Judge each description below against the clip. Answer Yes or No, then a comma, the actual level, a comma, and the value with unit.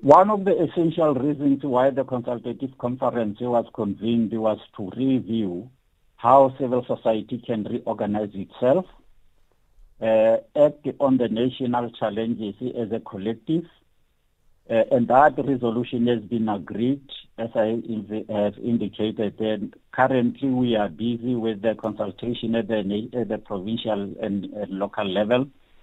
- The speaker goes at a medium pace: No, slow, 130 wpm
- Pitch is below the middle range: Yes, low, 115 Hz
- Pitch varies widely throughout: No, average, 2.8 semitones